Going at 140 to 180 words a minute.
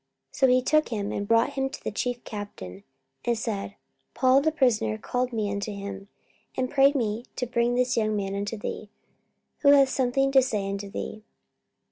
No: average, 190 wpm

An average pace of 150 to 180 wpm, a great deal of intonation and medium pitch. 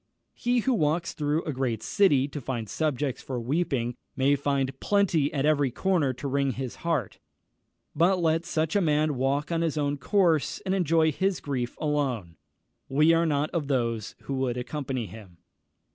No: average, 170 wpm; average, 4.0 semitones; medium, 145 Hz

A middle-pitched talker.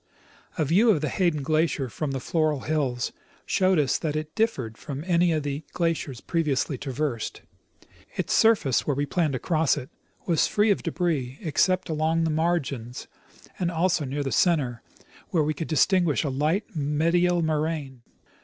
Yes: medium, 155 Hz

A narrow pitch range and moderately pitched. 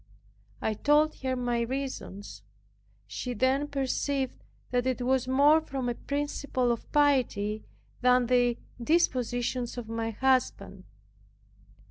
No: narrow, 2.3 semitones; very high, 255 Hz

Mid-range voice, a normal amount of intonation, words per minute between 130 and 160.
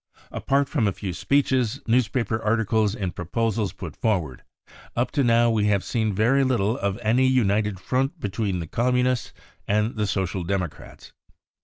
No: low, 110 Hz; average, 4.0 semitones; average, 155 wpm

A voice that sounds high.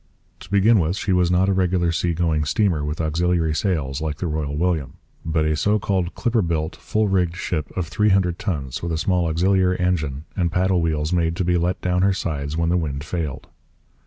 No: very low, 85 Hz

